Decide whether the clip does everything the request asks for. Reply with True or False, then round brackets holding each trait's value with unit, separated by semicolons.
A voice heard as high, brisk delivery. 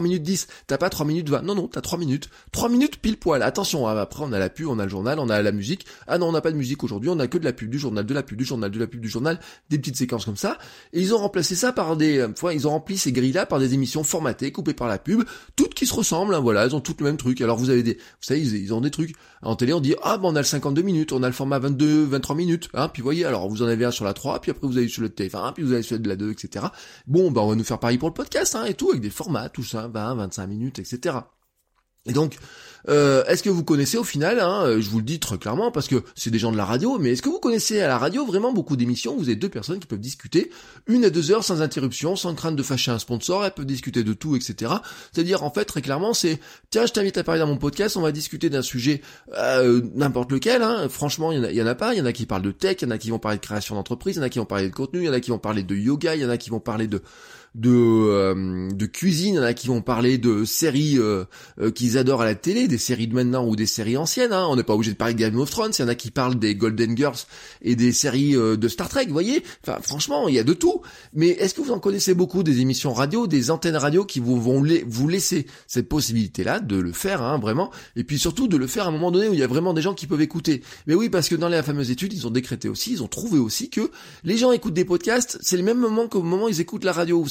False (140 Hz; 310 wpm)